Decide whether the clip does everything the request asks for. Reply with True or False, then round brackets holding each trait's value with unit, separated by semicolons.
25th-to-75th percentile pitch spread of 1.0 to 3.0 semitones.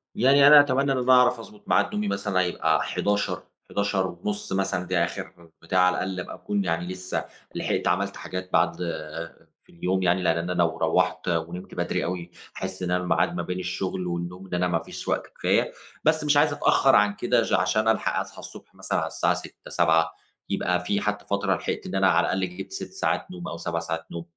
True (2.7 semitones)